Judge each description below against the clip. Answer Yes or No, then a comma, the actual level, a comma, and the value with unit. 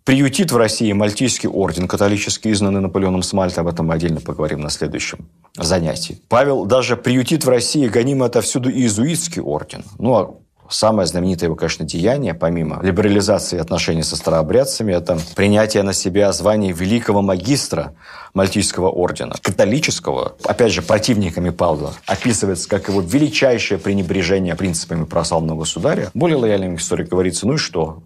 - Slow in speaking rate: No, average, 145 wpm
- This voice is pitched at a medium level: No, very low, 95 Hz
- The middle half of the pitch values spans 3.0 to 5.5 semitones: Yes, average, 4.2 semitones